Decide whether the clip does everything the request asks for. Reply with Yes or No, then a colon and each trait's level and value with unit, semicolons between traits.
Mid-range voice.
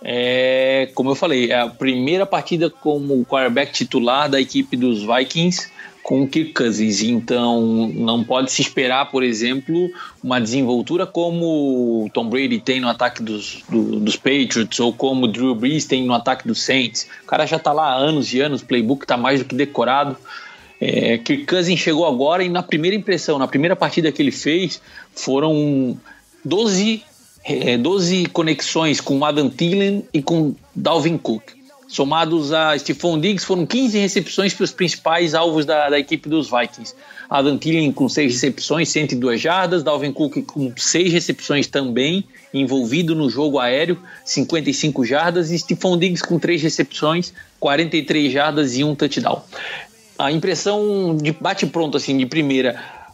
Yes: medium, 150 Hz